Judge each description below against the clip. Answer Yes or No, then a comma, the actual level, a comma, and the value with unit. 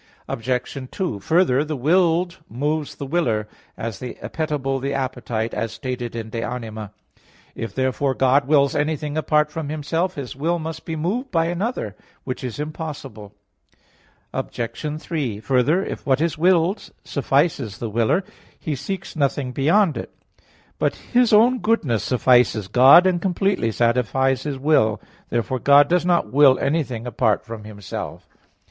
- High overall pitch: No, medium, 140 Hz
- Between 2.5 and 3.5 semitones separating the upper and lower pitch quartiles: No, average, 5.2 semitones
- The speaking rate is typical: Yes, average, 155 wpm